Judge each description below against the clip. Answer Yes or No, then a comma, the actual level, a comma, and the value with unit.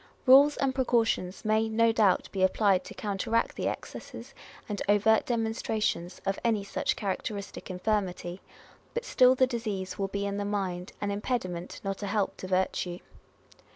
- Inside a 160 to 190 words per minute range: Yes, average, 165 wpm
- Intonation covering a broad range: No, average, 2.9 semitones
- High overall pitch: Yes, high, 205 Hz